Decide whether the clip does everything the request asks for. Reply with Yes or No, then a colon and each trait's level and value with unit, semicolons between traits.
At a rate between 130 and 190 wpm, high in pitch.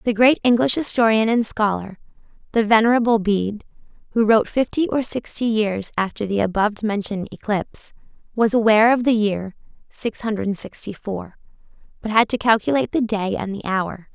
Yes: average, 160 wpm; high, 215 Hz